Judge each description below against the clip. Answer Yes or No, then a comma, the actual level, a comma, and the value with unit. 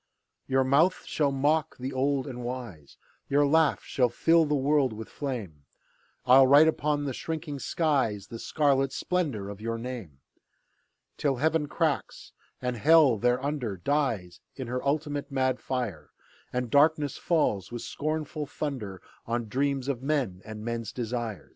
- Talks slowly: No, average, 150 wpm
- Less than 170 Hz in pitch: Yes, low, 135 Hz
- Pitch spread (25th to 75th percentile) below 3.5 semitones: No, average, 4.0 semitones